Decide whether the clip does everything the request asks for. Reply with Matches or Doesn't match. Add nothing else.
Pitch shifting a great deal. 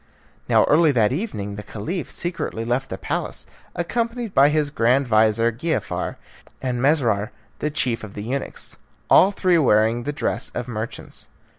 Matches